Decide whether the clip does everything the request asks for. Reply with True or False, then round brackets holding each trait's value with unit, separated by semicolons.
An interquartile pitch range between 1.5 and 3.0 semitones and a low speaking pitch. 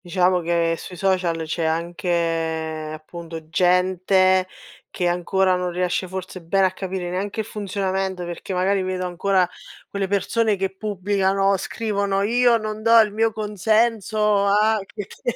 False (2.4 semitones; 190 Hz)